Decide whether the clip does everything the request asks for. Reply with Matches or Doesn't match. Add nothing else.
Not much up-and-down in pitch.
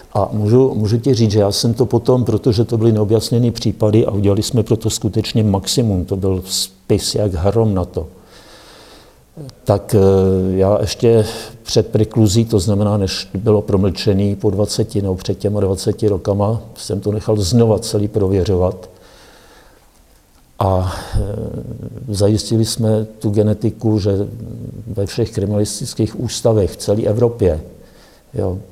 Matches